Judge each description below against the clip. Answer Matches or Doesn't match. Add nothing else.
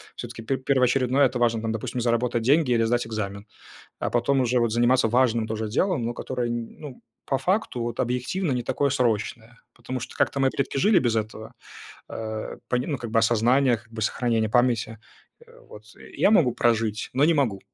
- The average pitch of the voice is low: Matches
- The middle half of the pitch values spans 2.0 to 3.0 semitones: Matches